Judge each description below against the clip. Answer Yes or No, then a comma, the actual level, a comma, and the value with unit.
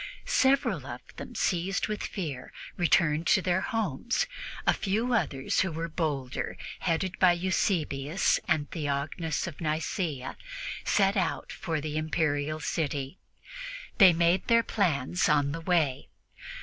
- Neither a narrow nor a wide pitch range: Yes, average, 4.2 semitones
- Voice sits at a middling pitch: Yes, medium, 165 Hz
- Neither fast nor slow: No, slow, 130 wpm